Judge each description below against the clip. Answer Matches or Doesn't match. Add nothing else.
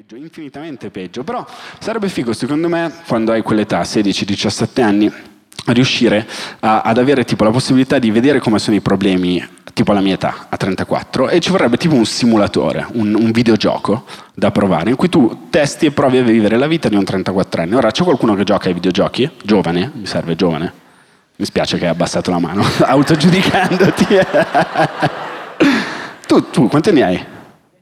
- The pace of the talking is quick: Matches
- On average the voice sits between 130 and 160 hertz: Doesn't match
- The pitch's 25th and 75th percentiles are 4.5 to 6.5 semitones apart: Matches